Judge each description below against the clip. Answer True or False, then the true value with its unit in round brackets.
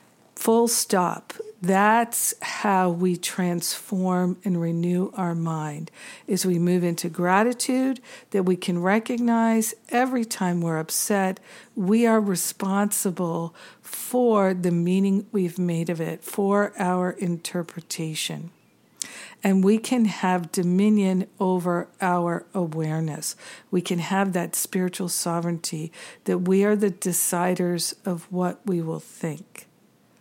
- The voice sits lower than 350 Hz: True (185 Hz)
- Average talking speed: False (120 wpm)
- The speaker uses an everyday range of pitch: True (3.0 semitones)